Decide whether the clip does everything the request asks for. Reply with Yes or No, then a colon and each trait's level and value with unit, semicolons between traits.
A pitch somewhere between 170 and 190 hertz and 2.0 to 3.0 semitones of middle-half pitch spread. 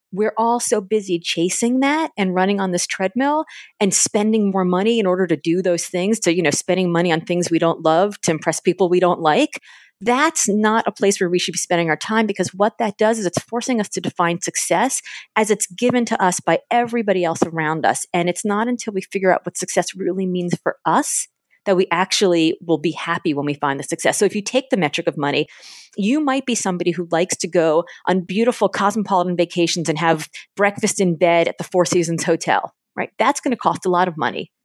No: medium, 185 Hz; average, 4.1 semitones